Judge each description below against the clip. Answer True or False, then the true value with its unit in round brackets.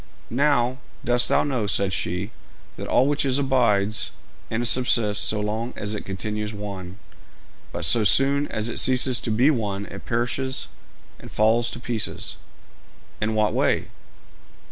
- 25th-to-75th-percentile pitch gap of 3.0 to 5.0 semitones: True (3.5 semitones)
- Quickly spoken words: False (150 wpm)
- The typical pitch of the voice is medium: False (115 Hz)